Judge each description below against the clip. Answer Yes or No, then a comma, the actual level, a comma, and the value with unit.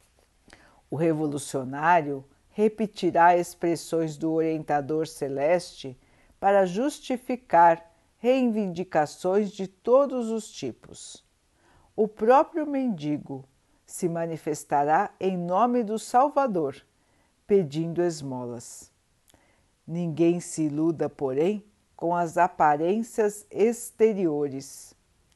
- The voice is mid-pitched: Yes, medium, 170 Hz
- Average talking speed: No, slow, 80 wpm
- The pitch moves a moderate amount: No, wide, 6.3 semitones